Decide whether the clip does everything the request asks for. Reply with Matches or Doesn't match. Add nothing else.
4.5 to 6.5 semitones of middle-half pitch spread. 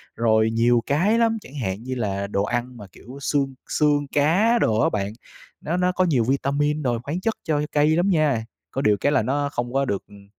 Matches